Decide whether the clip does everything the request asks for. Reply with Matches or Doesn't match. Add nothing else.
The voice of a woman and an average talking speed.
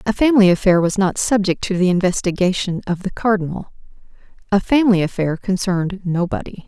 Matches